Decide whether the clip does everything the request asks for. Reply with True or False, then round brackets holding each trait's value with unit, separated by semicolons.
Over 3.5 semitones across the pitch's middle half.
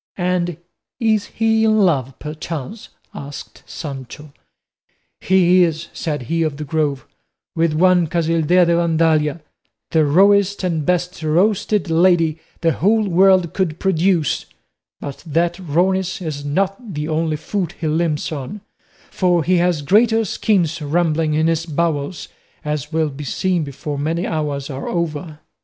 False (3.2 semitones)